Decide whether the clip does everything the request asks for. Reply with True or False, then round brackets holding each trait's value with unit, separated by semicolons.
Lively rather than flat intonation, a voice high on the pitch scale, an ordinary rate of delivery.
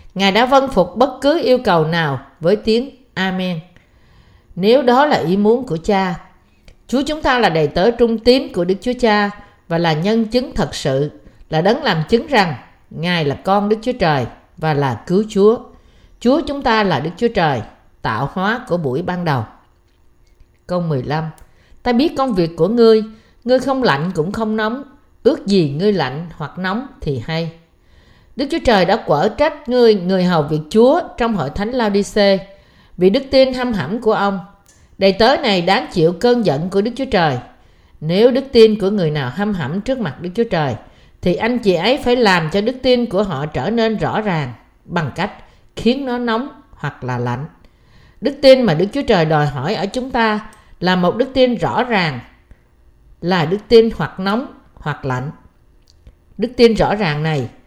True (6.8 semitones; 200 Hz; 190 wpm)